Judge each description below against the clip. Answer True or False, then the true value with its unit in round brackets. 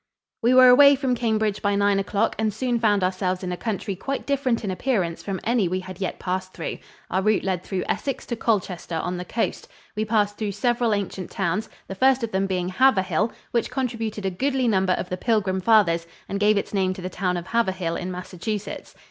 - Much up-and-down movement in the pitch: False (3.7 semitones)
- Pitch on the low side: False (200 Hz)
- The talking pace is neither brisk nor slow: False (215 wpm)